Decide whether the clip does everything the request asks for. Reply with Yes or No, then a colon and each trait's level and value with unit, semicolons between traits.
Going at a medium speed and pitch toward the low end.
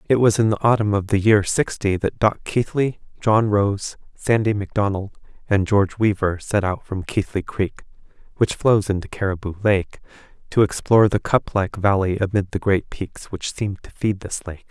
Yes: average, 185 wpm; low, 100 Hz